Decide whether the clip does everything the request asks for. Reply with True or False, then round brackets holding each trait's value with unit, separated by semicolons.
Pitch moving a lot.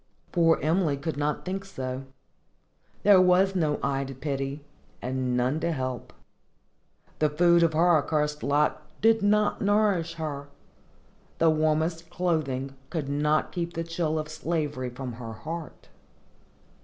False (3.5 semitones)